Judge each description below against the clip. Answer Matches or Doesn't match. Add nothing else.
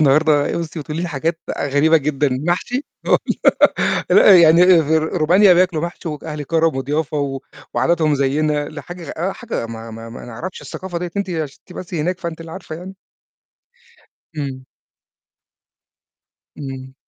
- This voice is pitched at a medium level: Matches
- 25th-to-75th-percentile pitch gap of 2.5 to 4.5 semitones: Matches